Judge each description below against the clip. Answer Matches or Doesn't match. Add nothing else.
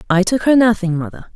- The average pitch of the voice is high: Matches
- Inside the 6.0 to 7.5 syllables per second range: Matches